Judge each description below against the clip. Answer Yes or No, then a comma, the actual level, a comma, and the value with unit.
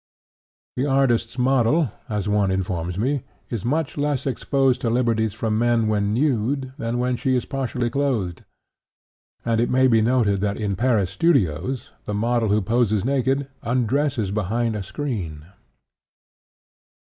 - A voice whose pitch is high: No, low, 115 Hz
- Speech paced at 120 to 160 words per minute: Yes, average, 145 wpm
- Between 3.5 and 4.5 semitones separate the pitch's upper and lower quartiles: Yes, average, 3.9 semitones